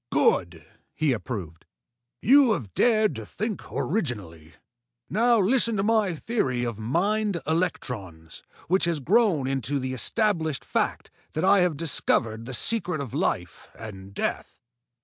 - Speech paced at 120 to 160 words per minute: Yes, slow, 135 wpm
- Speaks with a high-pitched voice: No, medium, 155 Hz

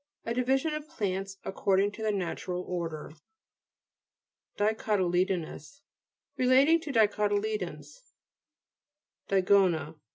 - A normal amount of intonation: Yes, average, 4.3 semitones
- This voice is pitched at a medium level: No, high, 205 Hz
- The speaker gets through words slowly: Yes, slow, 95 wpm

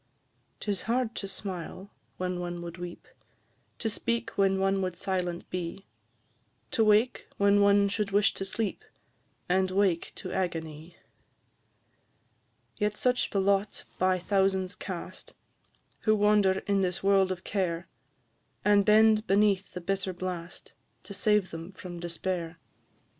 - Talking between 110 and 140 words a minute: Yes, slow, 135 wpm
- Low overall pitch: No, high, 195 Hz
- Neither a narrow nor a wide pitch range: No, narrow, 2.2 semitones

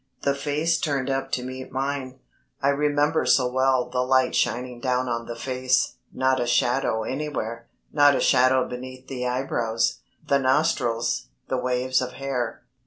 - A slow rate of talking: No, average, 160 wpm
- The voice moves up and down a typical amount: No, narrow, 1.7 semitones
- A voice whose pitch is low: Yes, low, 130 Hz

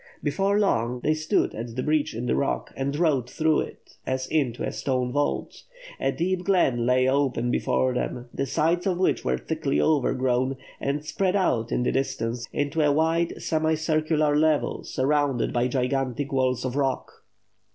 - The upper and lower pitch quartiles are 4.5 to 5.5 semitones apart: No, average, 3.7 semitones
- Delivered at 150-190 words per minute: Yes, average, 170 wpm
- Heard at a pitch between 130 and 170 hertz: Yes, medium, 140 Hz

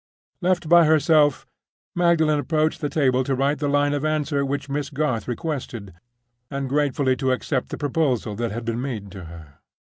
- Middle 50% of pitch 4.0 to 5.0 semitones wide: No, average, 3.3 semitones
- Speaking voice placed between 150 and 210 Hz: No, medium, 140 Hz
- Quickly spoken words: No, average, 175 wpm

